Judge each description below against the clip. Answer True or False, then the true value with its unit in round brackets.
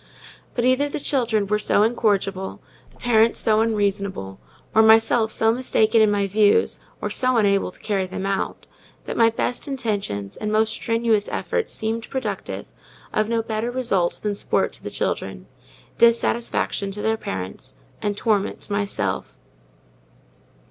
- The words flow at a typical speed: True (150 wpm)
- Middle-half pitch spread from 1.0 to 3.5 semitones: True (2.4 semitones)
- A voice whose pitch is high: True (220 Hz)